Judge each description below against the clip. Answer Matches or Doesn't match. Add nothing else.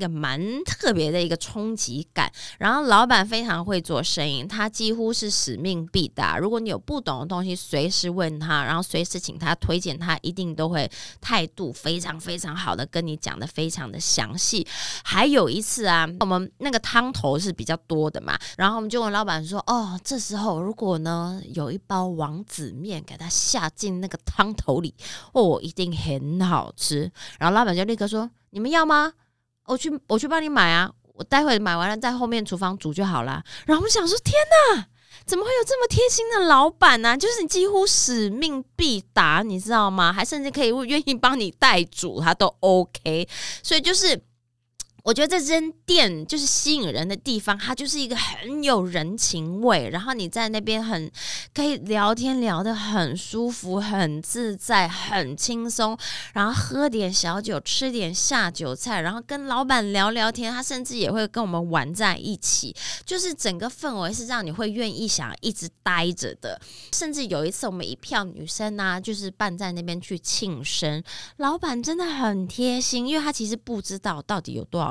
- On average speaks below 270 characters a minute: Doesn't match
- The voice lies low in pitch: Doesn't match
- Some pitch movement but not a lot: Doesn't match